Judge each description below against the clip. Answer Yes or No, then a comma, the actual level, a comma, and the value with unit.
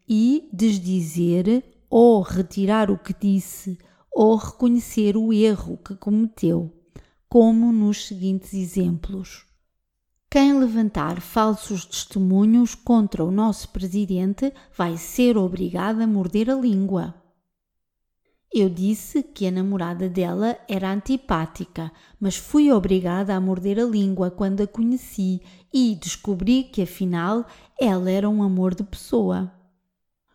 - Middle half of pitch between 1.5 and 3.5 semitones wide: Yes, average, 3.2 semitones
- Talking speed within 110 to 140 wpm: Yes, slow, 120 wpm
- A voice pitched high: Yes, high, 195 Hz